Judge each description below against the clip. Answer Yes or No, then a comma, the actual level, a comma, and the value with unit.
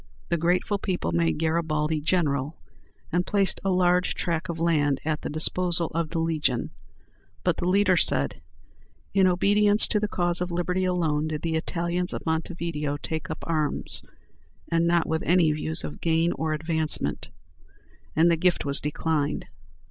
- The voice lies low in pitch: No, medium, 165 Hz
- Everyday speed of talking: Yes, average, 160 wpm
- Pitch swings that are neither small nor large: No, narrow, 2.3 semitones